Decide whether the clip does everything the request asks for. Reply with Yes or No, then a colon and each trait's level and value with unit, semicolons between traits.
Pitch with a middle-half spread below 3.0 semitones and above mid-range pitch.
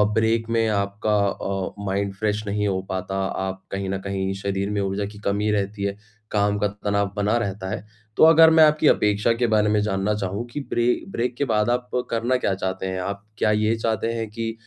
No: narrow, 2.4 semitones; low, 105 Hz